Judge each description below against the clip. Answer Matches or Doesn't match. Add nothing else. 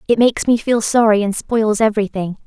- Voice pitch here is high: Matches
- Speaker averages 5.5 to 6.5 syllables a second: Matches